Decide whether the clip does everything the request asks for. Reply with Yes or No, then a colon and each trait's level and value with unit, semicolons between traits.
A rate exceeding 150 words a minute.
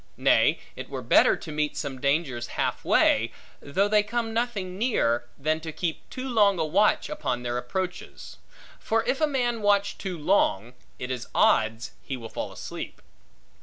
Yes: average, 170 wpm